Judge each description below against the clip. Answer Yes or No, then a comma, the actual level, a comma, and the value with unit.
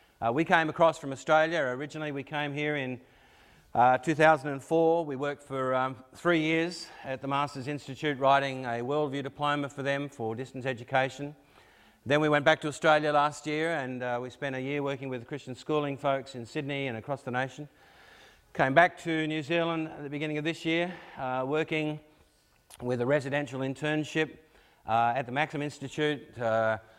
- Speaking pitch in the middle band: Yes, medium, 145 Hz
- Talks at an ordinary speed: Yes, average, 180 wpm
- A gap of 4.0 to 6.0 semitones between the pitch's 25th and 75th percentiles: No, average, 2.7 semitones